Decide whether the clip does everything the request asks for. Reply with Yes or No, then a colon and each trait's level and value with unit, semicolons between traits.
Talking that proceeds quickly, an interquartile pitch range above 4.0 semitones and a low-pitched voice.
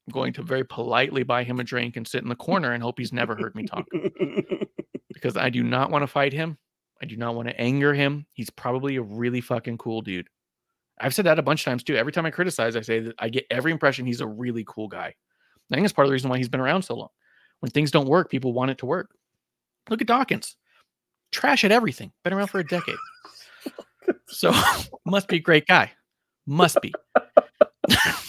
Yes: fast, 230 wpm; average, 5.0 semitones; low, 130 Hz